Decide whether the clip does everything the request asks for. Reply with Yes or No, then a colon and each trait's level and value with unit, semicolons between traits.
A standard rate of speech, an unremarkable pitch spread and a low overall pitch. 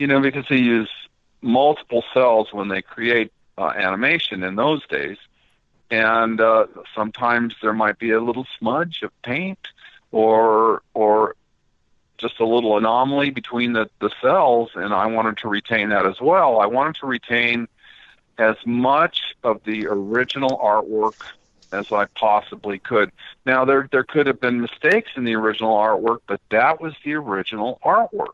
Yes: average, 160 wpm; average, 3.0 semitones; low, 115 Hz